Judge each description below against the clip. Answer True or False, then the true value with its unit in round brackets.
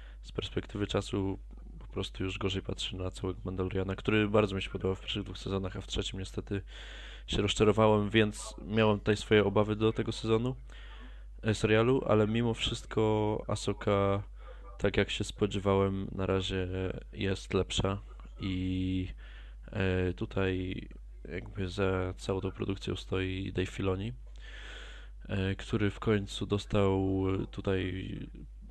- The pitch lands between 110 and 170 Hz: False (100 Hz)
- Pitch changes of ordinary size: False (2.1 semitones)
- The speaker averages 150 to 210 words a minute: False (135 wpm)